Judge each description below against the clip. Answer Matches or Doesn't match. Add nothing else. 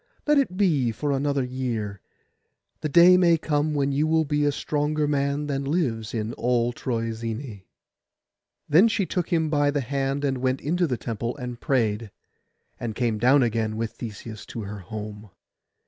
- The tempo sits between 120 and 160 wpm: Doesn't match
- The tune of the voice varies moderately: Matches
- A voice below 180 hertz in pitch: Matches